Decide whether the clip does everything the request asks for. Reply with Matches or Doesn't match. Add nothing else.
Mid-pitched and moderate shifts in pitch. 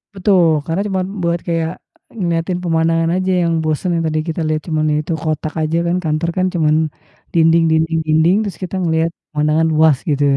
Doesn't match